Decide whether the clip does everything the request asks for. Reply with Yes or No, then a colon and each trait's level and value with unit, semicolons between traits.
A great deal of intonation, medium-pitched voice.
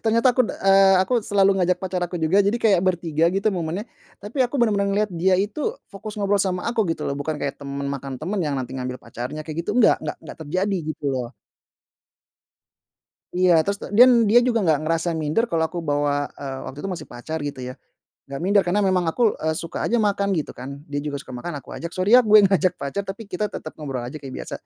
Yes: wide, 5.7 semitones; medium, 180 Hz